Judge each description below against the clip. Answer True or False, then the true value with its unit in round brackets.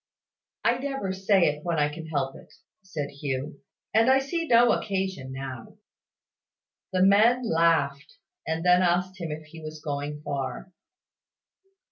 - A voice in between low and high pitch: True (165 Hz)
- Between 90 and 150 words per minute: True (145 wpm)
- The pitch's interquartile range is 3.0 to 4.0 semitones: False (5.0 semitones)